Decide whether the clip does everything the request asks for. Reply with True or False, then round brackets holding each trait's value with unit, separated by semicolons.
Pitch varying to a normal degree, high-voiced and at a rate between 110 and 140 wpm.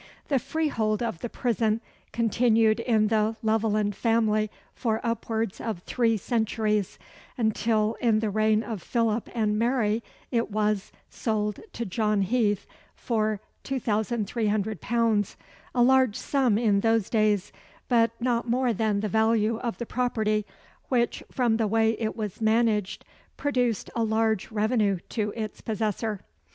False (1.6 semitones; 220 Hz; 135 wpm)